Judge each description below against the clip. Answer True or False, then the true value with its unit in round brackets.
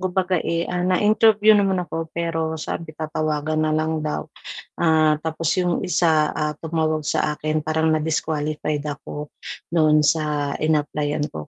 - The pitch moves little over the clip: True (1.7 semitones)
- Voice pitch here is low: False (155 Hz)